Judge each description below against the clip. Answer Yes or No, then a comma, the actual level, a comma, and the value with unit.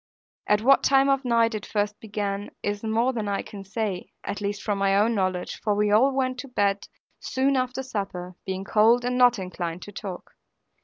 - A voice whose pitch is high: Yes, high, 210 Hz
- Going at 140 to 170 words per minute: No, average, 200 wpm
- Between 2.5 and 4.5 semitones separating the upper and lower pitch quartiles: Yes, average, 3.8 semitones